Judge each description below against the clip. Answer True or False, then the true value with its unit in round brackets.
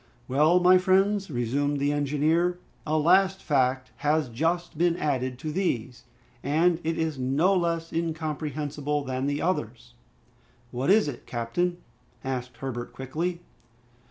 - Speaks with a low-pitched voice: False (150 Hz)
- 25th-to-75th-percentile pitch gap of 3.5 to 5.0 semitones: True (4.6 semitones)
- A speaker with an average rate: False (130 wpm)